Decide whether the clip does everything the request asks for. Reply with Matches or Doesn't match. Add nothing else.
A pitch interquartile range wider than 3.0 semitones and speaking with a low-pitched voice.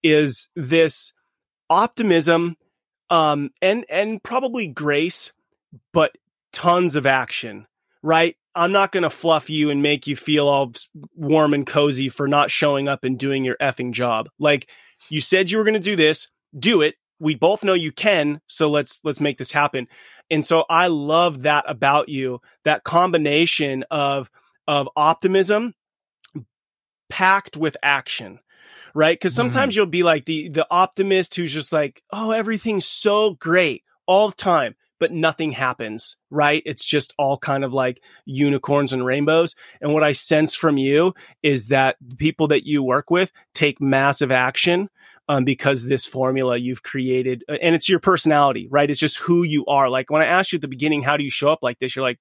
Doesn't match